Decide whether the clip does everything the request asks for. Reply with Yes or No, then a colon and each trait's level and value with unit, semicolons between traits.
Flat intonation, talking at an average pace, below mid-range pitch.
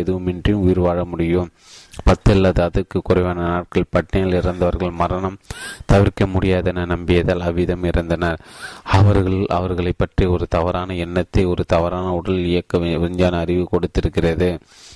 Yes: narrow, 1.2 semitones; average, 115 wpm; very low, 90 Hz